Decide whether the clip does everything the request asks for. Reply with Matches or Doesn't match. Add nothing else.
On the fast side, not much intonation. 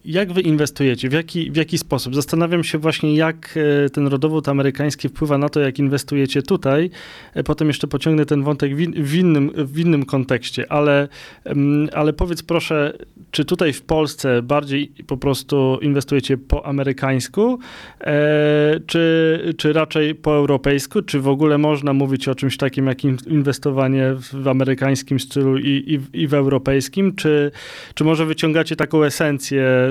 Doesn't match